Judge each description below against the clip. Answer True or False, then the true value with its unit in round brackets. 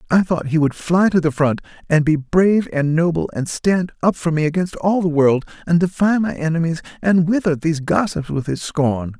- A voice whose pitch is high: False (165 Hz)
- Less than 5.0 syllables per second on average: False (5.1 syllables/s)